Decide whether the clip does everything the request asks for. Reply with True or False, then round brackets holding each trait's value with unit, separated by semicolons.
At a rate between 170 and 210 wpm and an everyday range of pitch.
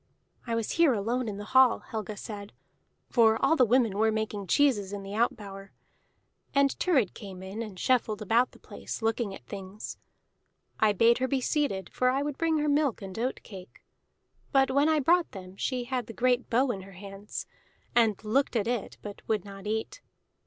True (195 wpm; 4.3 semitones)